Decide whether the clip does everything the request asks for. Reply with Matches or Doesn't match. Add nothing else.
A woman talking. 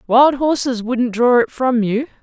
Matches